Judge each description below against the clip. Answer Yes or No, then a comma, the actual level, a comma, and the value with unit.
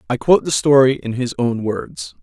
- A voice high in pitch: No, low, 125 Hz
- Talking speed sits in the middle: No, fast, 215 wpm